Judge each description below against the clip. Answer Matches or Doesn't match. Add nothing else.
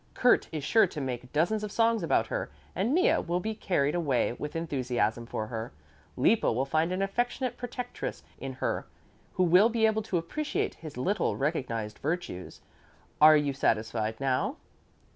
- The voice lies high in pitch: Doesn't match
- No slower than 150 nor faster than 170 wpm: Matches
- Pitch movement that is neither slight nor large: Doesn't match